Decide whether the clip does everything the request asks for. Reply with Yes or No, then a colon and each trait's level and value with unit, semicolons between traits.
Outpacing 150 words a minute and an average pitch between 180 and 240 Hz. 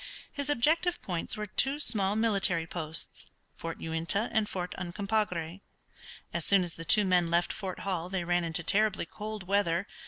Yes: average, 165 wpm; high, 190 Hz